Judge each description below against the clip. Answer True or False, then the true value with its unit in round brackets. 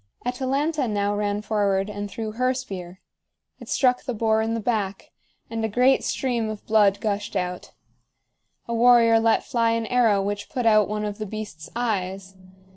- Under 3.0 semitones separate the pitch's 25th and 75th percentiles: True (2.6 semitones)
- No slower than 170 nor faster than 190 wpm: True (175 wpm)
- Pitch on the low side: False (215 Hz)